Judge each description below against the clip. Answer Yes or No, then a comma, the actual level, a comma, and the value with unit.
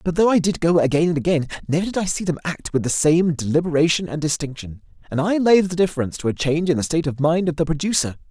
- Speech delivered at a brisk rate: Yes, fast, 260 wpm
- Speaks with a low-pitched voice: No, medium, 160 Hz